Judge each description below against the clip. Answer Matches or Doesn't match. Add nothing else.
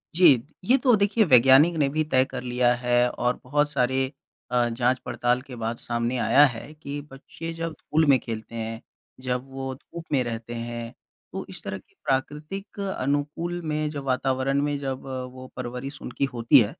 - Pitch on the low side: Matches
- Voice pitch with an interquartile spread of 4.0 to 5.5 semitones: Doesn't match